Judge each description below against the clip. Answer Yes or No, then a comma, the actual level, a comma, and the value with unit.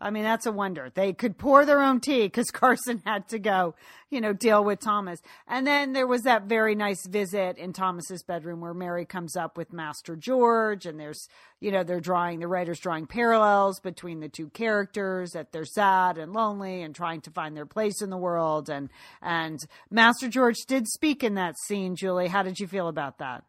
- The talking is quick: Yes, fast, 210 wpm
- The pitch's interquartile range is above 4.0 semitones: Yes, average, 4.4 semitones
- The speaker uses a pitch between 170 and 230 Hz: Yes, high, 190 Hz